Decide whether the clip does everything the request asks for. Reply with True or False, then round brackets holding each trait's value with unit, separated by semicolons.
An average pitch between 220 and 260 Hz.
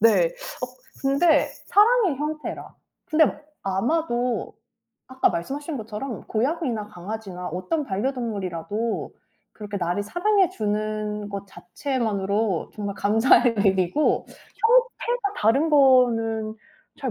True (230 Hz)